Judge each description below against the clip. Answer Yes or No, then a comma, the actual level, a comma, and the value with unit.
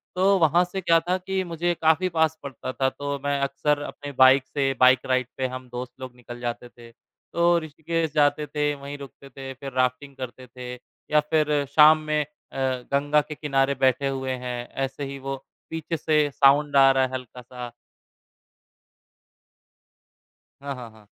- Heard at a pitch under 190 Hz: Yes, medium, 140 Hz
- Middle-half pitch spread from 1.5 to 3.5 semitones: Yes, average, 2.8 semitones